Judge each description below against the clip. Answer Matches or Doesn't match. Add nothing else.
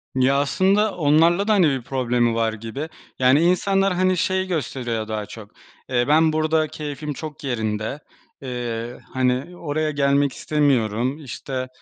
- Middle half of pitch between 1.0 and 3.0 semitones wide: Doesn't match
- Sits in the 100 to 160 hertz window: Matches